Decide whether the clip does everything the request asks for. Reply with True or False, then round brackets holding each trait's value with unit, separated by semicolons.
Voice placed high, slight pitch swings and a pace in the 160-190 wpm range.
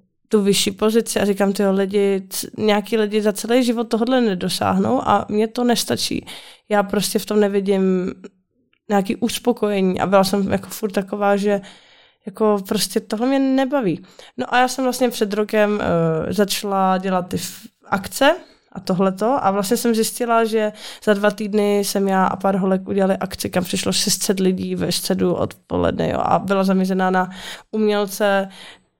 True (205 Hz; 2.3 semitones; 165 wpm)